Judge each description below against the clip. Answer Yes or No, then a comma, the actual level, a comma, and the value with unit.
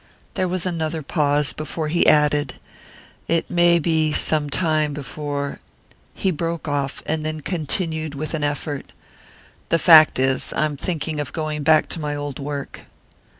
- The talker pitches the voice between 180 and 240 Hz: No, medium, 155 Hz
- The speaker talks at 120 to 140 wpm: No, average, 160 wpm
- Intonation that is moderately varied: No, narrow, 1.9 semitones